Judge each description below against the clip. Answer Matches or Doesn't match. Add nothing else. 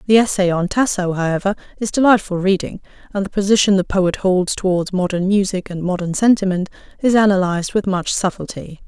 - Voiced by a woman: Matches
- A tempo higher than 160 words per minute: Matches